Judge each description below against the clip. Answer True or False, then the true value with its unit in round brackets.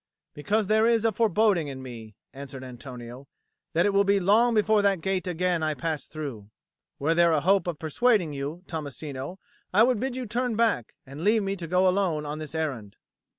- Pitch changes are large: True (6.1 semitones)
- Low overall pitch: False (170 Hz)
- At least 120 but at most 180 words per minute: False (195 wpm)